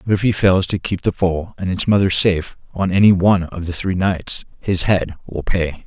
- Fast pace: Yes, fast, 235 wpm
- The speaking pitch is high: No, very low, 90 Hz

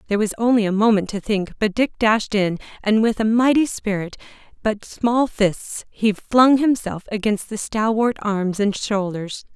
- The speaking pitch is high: Yes, high, 215 Hz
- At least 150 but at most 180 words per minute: Yes, average, 175 wpm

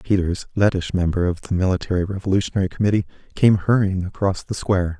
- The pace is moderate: Yes, average, 155 wpm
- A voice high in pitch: No, very low, 95 Hz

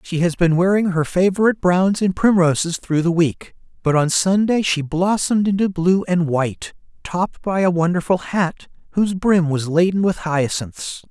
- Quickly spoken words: No, average, 175 wpm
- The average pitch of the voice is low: No, medium, 175 Hz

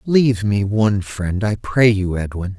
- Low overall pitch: Yes, low, 105 Hz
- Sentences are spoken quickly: No, average, 185 wpm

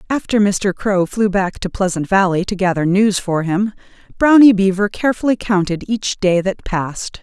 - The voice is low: No, high, 195 Hz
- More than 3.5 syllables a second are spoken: Yes, 4.9 syllables/s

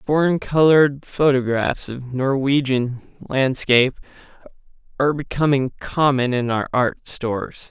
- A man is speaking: Yes, male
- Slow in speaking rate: Yes, slow, 100 wpm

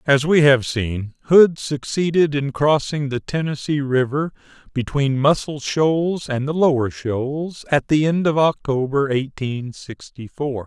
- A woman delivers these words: No, male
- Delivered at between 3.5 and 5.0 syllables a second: Yes, 4.0 syllables/s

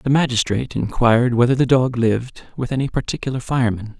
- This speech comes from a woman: No, male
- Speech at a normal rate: Yes, average, 165 wpm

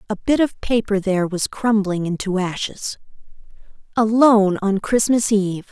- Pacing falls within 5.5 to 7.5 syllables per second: No, 5.0 syllables/s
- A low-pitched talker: No, high, 210 Hz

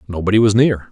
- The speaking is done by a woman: No, male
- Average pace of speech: Yes, average, 195 wpm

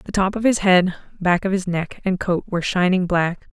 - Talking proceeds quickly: Yes, fast, 235 wpm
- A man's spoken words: No, female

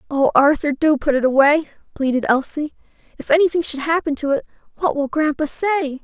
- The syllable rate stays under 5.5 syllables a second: No, 5.6 syllables/s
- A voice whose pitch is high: Yes, very high, 295 Hz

